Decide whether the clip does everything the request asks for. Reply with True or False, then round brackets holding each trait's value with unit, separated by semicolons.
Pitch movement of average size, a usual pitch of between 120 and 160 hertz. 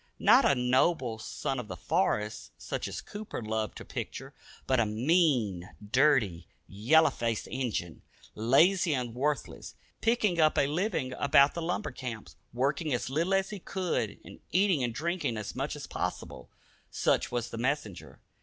False (6.4 semitones; 135 Hz)